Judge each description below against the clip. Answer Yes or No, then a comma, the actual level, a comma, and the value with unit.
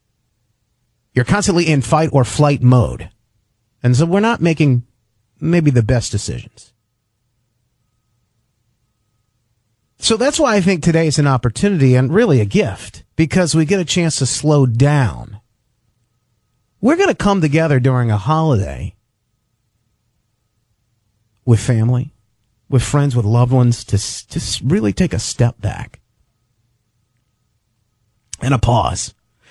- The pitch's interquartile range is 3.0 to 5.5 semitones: Yes, average, 3.3 semitones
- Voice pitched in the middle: No, low, 120 Hz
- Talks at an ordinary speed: No, slow, 125 wpm